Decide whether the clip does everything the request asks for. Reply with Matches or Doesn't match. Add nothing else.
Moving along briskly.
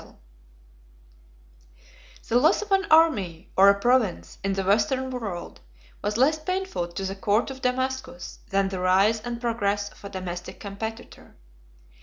Doesn't match